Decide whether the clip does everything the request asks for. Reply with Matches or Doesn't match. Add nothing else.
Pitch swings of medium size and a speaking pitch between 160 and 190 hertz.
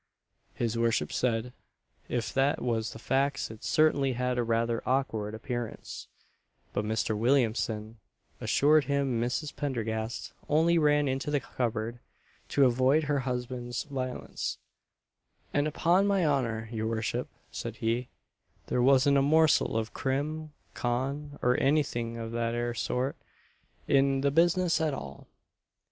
Doesn't match